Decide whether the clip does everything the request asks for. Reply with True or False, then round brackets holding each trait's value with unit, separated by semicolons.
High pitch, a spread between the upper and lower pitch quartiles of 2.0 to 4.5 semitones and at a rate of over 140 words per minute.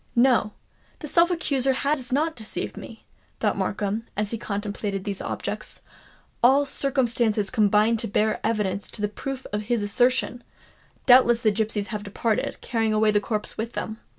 True (225 Hz; 3.3 semitones; 155 wpm)